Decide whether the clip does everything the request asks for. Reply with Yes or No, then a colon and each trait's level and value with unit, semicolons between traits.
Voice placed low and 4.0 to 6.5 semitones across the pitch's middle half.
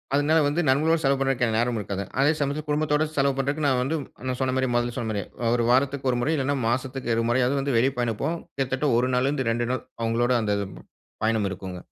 No: low, 130 Hz; average, 3.0 semitones